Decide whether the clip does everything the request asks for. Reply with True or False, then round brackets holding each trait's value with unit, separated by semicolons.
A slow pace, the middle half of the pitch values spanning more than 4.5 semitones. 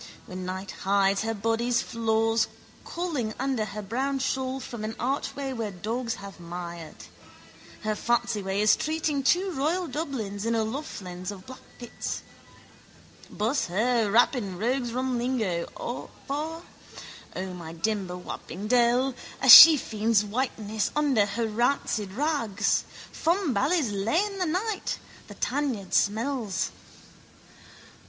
True (120 wpm; 5.0 semitones)